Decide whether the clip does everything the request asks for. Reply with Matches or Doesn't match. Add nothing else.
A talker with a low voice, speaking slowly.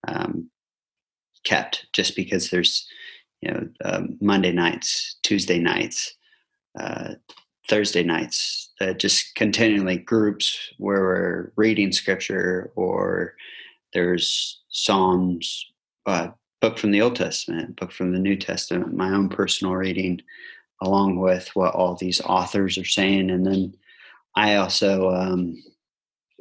Matches